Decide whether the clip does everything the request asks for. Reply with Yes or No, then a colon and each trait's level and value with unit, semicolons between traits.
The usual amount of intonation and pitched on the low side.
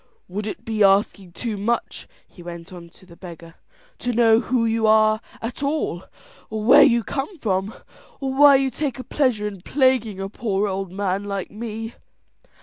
No: average, 3.8 semitones; high, 215 Hz